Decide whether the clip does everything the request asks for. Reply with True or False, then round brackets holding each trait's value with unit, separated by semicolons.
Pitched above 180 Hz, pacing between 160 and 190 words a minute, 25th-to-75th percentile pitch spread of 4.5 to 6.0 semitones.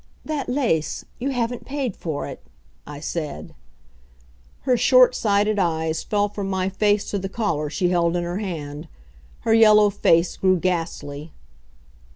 False (190 Hz; 150 wpm; 5.1 semitones)